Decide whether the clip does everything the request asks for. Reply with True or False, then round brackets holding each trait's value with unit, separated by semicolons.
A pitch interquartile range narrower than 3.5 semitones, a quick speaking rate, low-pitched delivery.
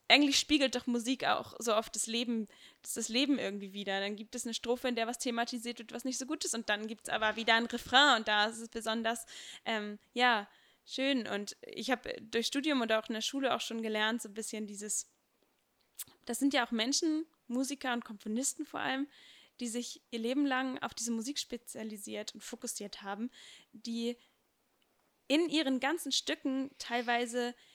False (2.9 semitones; 195 wpm; 240 Hz)